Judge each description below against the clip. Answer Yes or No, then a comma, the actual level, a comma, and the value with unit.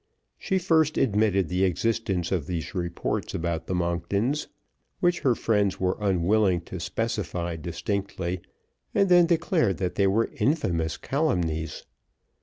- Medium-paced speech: No, slow, 130 wpm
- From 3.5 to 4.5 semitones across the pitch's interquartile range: No, average, 5.1 semitones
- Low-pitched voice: Yes, very low, 95 Hz